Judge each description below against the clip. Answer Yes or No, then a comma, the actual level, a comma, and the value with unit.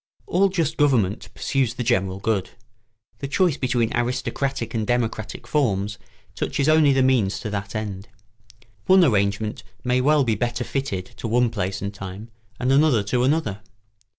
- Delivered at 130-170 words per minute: Yes, average, 160 wpm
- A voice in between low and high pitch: No, low, 120 Hz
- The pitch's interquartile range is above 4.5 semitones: Yes, average, 5.0 semitones